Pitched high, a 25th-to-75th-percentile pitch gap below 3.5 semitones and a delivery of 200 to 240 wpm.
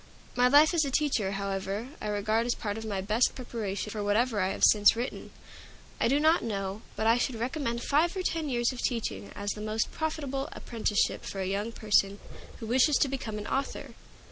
No: high, 225 Hz; average, 4.4 semitones; fast, 205 wpm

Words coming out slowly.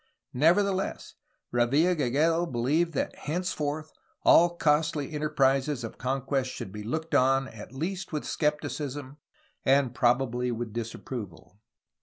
Yes: slow, 120 wpm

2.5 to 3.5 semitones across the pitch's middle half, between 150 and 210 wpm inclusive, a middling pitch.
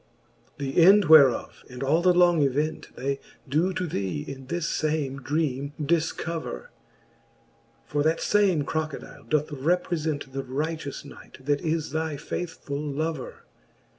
No: average, 2.9 semitones; slow, 135 wpm; medium, 150 Hz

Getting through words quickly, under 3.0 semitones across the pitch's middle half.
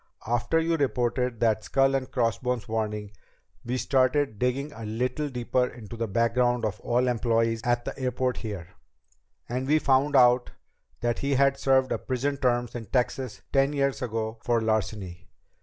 No: average, 160 wpm; narrow, 2.6 semitones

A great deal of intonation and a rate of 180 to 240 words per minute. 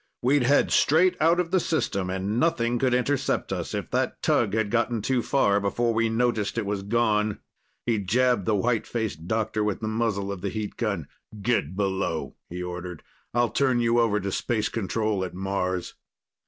No: average, 3.5 semitones; average, 185 wpm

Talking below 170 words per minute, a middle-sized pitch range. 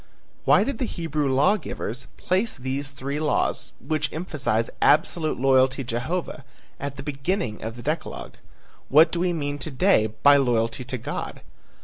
Yes: average, 160 wpm; average, 3.5 semitones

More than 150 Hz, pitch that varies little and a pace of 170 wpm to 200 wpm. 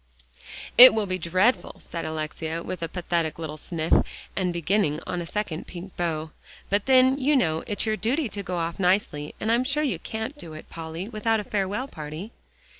No: medium, 185 Hz; average, 5.3 semitones; average, 190 wpm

